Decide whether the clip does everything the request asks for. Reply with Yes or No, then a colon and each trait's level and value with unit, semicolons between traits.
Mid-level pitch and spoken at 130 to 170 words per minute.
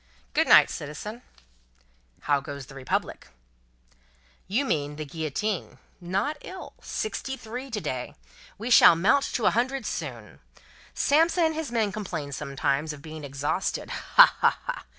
Yes: medium, 180 Hz; average, 145 wpm